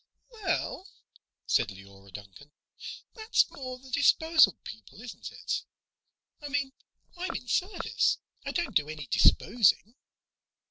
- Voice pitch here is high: Yes, very high, 250 Hz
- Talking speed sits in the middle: No, slow, 120 wpm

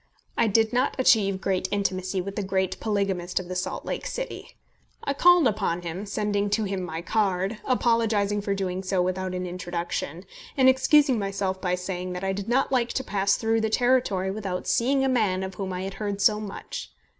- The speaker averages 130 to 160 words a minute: No, average, 200 wpm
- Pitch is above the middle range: Yes, high, 200 Hz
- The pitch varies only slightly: No, average, 3.1 semitones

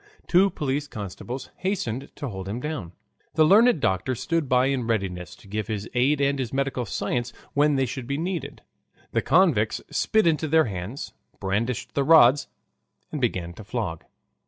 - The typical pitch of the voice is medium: No, low, 130 Hz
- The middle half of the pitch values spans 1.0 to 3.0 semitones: No, wide, 5.6 semitones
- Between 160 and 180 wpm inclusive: Yes, average, 170 wpm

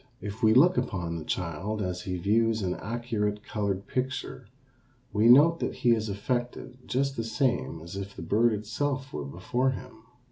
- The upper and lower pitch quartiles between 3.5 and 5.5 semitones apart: Yes, average, 4.2 semitones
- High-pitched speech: No, low, 110 Hz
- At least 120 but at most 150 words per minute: No, average, 175 wpm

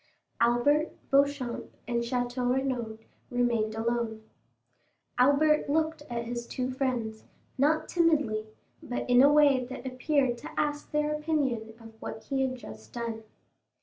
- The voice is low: No, very high, 250 Hz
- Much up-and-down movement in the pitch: No, average, 3.4 semitones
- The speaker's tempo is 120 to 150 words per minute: Yes, slow, 135 wpm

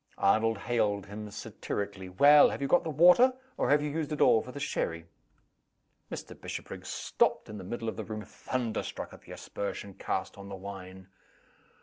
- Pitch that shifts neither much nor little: No, wide, 6.2 semitones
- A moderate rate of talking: Yes, average, 190 wpm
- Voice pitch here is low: Yes, low, 110 Hz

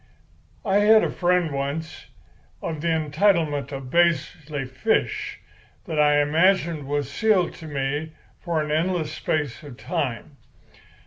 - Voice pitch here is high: No, medium, 155 Hz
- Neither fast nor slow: No, slow, 130 wpm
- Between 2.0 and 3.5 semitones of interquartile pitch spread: Yes, average, 3.1 semitones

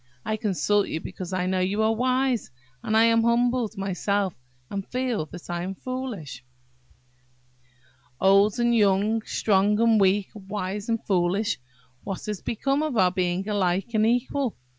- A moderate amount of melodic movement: Yes, average, 3.6 semitones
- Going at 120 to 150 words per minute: Yes, average, 140 wpm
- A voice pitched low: No, high, 205 Hz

